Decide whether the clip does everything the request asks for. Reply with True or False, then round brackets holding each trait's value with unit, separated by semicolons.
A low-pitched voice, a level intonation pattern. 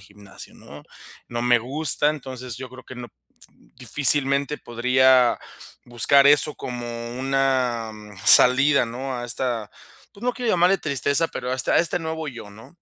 False (130 Hz; 3.0 semitones)